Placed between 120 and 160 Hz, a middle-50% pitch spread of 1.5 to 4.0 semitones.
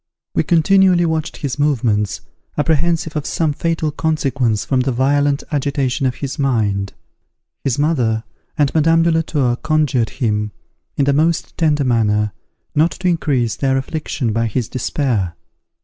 No: medium, 140 Hz; average, 4.7 semitones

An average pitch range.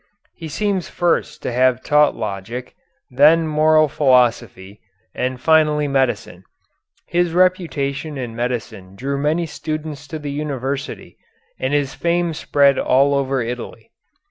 Yes: average, 3.7 semitones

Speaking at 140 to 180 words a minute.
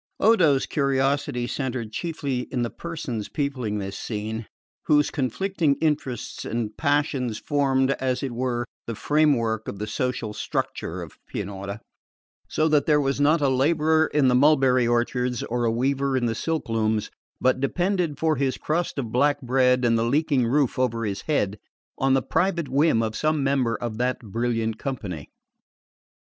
Yes: average, 160 wpm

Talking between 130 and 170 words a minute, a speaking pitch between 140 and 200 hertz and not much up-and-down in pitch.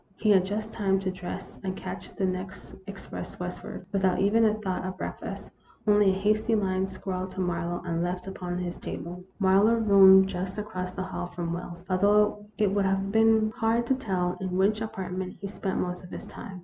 No: average, 200 wpm; high, 190 Hz; narrow, 2.2 semitones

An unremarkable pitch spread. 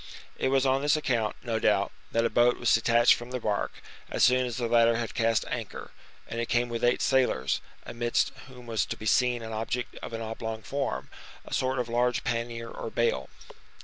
No: narrow, 1.6 semitones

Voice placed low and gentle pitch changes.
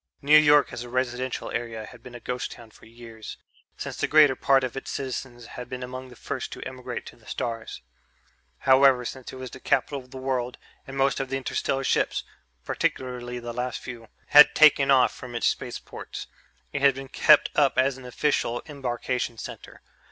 Yes: low, 130 Hz; narrow, 1.9 semitones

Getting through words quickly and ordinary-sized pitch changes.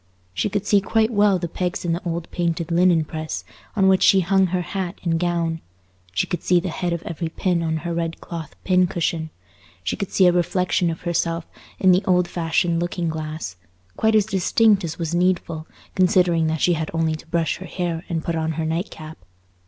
No: fast, 210 wpm; narrow, 2.1 semitones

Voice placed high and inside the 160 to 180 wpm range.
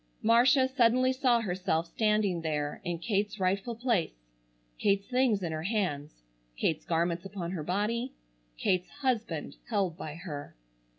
No: high, 195 Hz; slow, 135 wpm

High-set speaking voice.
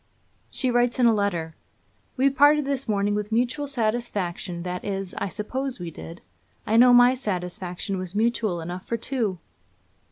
Yes: high, 215 Hz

